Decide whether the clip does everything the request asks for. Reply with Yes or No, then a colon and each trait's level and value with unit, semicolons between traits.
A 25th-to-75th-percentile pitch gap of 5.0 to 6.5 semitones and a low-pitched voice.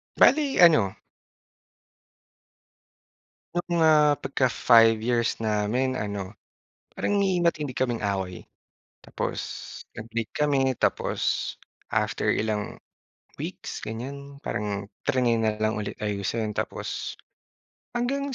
Yes: wide, 5.5 semitones; low, 120 Hz